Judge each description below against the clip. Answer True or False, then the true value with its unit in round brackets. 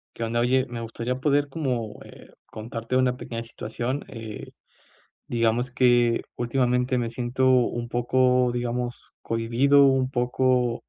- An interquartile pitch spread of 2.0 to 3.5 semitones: False (1.6 semitones)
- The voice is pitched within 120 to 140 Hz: True (125 Hz)